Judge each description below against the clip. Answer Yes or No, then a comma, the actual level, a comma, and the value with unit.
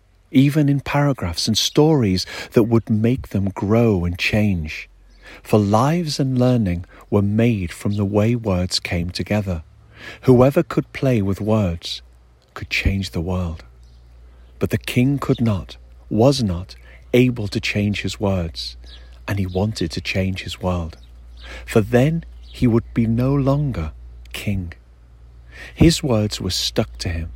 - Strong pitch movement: Yes, wide, 6.1 semitones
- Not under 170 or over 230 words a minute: No, average, 145 wpm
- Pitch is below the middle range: Yes, low, 100 Hz